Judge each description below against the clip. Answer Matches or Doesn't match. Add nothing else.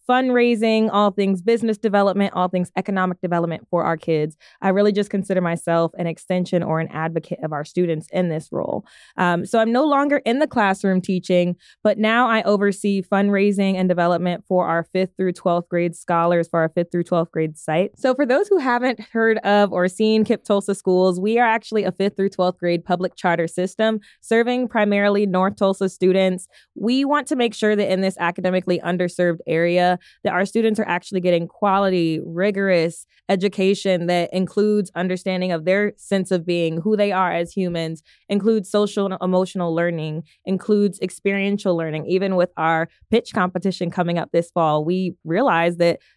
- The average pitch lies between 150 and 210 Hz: Matches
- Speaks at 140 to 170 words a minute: Doesn't match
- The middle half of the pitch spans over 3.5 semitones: Doesn't match